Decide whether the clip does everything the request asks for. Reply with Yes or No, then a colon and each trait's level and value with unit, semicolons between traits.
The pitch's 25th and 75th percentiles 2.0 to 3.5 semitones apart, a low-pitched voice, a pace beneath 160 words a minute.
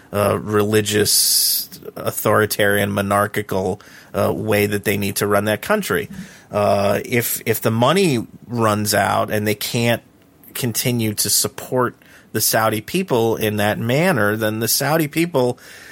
Yes: narrow, 2.6 semitones; low, 110 Hz; average, 140 wpm